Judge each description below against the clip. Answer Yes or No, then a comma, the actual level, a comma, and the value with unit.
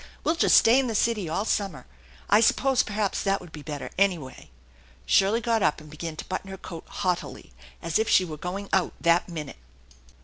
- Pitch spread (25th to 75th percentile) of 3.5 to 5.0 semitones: Yes, average, 4.6 semitones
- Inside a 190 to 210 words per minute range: Yes, average, 200 wpm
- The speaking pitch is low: No, high, 190 Hz